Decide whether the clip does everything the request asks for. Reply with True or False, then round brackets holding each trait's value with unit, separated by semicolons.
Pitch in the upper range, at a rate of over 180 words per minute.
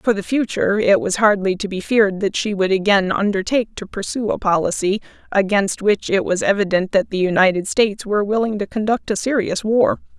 True (205 Hz; 200 wpm)